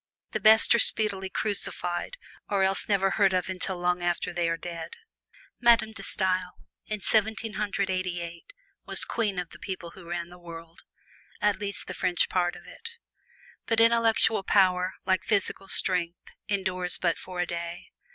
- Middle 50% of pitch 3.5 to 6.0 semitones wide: No, average, 2.9 semitones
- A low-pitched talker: No, medium, 185 Hz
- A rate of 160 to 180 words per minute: Yes, average, 170 wpm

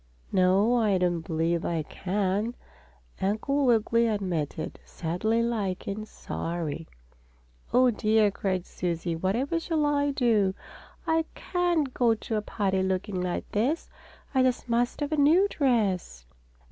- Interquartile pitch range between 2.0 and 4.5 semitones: No, wide, 5.5 semitones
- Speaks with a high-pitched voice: Yes, high, 215 Hz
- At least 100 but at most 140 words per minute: Yes, slow, 135 wpm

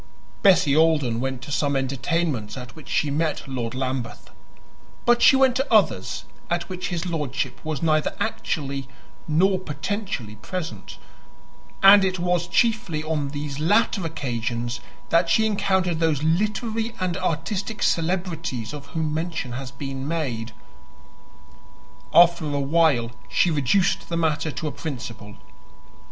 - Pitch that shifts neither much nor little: Yes, average, 4.8 semitones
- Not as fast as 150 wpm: Yes, slow, 135 wpm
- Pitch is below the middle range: No, medium, 160 Hz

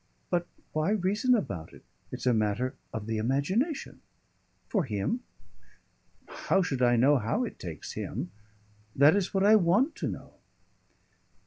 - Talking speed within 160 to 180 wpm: No, average, 150 wpm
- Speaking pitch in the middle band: Yes, medium, 155 Hz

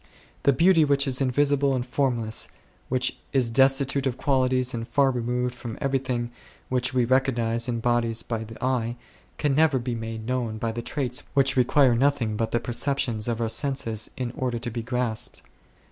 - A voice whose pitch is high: No, low, 125 Hz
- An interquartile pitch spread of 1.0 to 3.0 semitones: Yes, narrow, 2.5 semitones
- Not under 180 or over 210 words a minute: Yes, average, 185 wpm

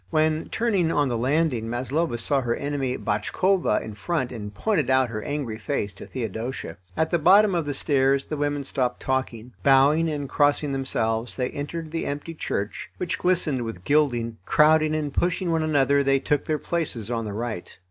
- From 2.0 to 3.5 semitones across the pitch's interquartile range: No, average, 4.7 semitones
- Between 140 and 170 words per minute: No, average, 185 wpm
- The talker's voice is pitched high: No, medium, 140 Hz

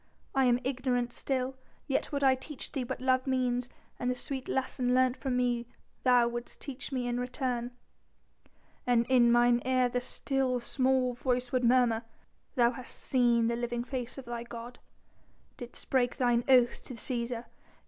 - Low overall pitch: No, very high, 250 Hz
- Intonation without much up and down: Yes, narrow, 1.3 semitones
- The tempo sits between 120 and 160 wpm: No, average, 170 wpm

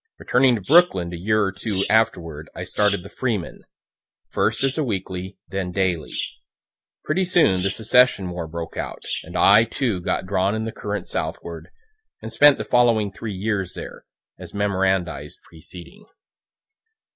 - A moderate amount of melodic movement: Yes, average, 3.8 semitones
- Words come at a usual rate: Yes, average, 155 wpm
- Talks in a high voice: No, low, 100 Hz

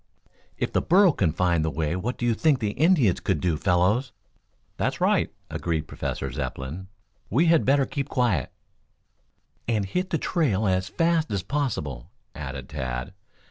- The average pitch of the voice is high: No, low, 100 Hz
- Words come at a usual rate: Yes, average, 165 wpm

